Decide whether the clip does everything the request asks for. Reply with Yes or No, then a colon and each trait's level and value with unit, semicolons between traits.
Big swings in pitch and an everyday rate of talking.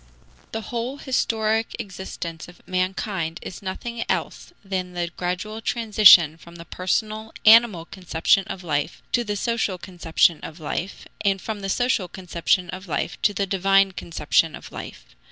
No: average, 3.8 semitones; average, 155 wpm